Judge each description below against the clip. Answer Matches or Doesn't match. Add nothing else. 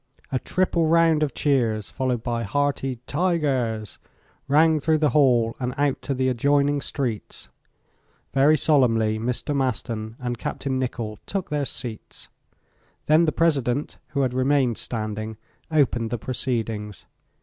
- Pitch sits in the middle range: Doesn't match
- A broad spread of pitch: Doesn't match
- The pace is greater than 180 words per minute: Doesn't match